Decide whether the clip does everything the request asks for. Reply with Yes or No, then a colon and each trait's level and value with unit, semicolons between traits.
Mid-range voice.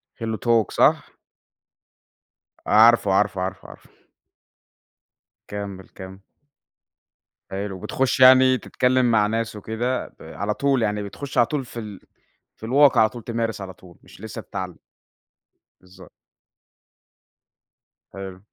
No: low, 110 Hz